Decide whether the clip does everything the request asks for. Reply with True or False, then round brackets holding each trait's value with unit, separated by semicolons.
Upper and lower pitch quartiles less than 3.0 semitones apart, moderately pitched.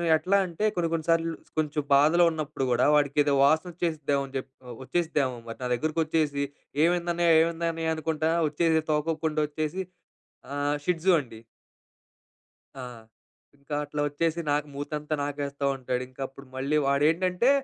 True (2.6 semitones; 155 Hz)